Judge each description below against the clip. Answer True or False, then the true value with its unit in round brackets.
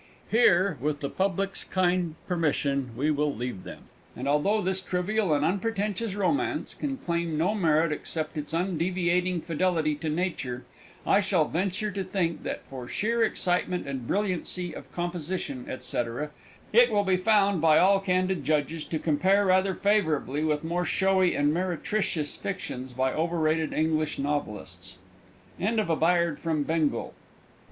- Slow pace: False (150 wpm)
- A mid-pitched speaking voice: True (170 Hz)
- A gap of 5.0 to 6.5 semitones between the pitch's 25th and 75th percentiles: False (4.0 semitones)